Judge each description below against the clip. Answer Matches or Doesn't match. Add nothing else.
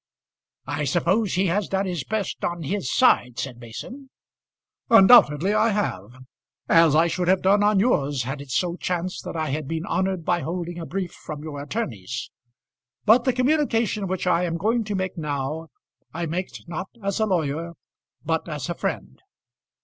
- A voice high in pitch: Doesn't match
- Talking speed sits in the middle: Matches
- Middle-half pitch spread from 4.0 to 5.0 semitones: Matches